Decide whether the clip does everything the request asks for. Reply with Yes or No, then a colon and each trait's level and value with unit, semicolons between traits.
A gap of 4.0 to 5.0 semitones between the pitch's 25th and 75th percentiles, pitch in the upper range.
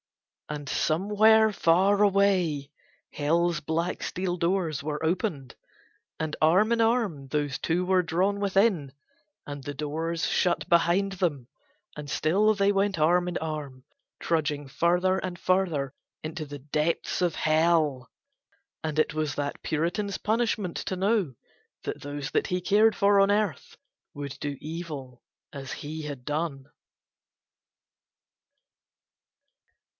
No: average, 4.6 semitones; medium, 165 Hz